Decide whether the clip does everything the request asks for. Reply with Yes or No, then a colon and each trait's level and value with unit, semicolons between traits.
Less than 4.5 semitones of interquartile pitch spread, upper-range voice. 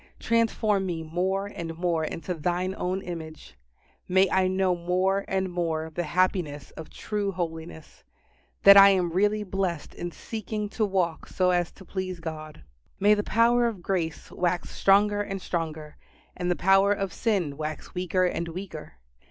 No: average, 2.8 semitones; medium, 180 Hz